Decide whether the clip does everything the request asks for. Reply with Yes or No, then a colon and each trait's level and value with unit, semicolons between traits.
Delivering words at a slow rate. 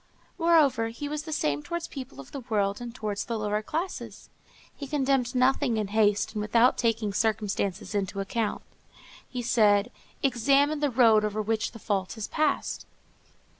No: average, 165 wpm